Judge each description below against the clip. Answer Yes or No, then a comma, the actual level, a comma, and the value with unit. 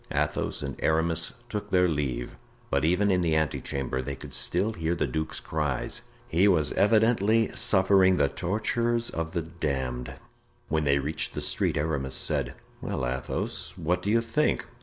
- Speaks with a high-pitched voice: No, very low, 80 Hz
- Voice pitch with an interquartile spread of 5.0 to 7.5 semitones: Yes, wide, 5.6 semitones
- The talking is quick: No, average, 165 wpm